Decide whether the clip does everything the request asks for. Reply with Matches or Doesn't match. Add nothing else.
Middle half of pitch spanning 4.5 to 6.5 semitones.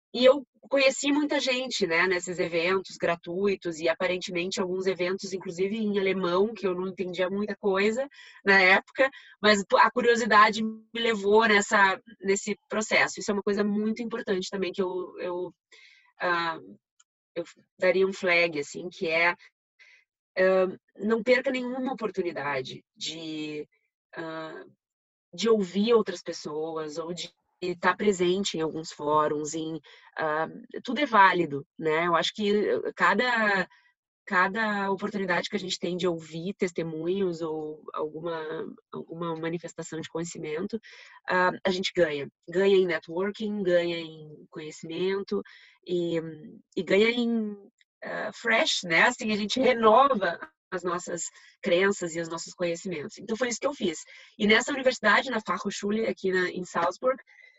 Doesn't match